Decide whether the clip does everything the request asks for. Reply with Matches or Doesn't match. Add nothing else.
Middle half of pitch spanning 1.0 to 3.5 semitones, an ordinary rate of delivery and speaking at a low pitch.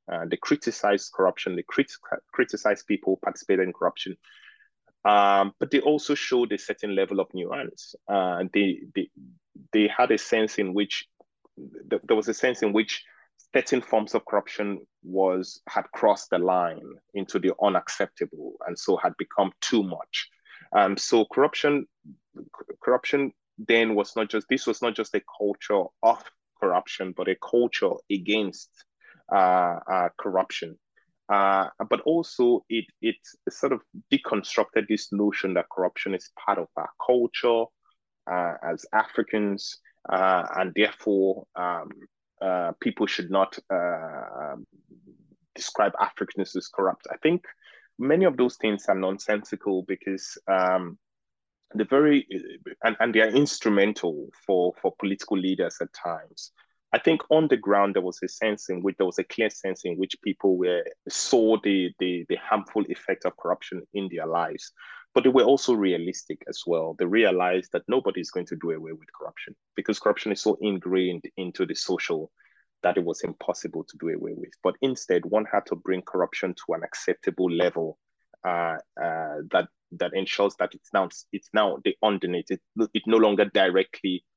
Doesn't match